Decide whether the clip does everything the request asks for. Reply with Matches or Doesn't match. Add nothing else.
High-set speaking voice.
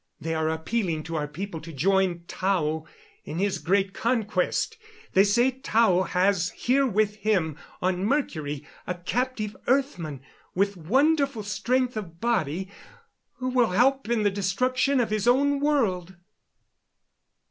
Matches